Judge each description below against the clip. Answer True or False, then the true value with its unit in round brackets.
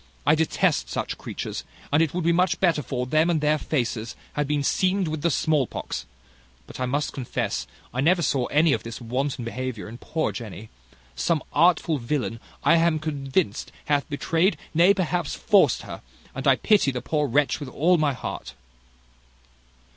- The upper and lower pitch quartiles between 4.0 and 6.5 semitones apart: True (4.4 semitones)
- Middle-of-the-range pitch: True (150 Hz)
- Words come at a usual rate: True (175 wpm)